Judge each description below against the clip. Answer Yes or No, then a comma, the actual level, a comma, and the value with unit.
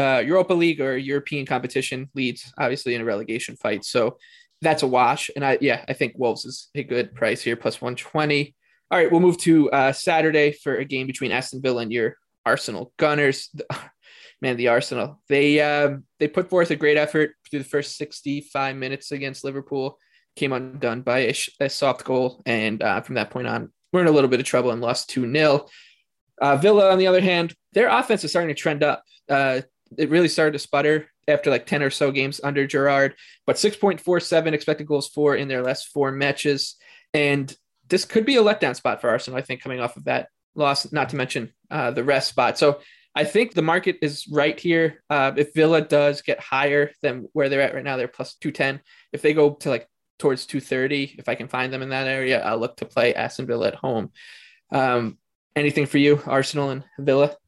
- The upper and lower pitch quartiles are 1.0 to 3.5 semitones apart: Yes, narrow, 2.5 semitones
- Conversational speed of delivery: No, fast, 210 wpm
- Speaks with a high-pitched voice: No, medium, 140 Hz